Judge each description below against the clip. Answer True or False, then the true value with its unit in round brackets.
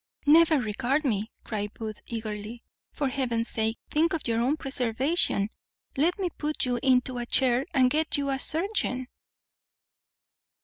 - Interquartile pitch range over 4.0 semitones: True (4.6 semitones)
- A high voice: True (255 Hz)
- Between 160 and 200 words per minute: False (145 wpm)